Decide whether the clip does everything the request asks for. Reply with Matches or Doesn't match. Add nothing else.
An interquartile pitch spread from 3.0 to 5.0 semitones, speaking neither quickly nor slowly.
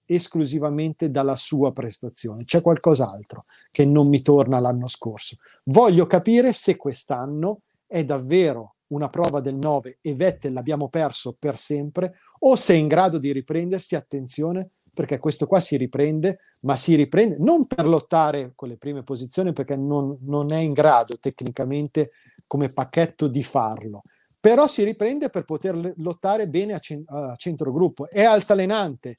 Matches